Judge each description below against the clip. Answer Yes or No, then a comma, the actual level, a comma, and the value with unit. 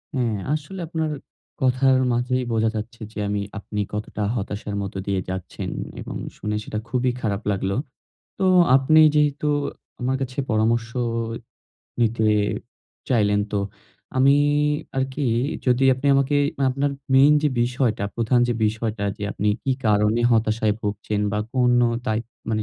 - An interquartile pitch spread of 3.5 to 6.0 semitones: Yes, average, 3.8 semitones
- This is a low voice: Yes, low, 120 Hz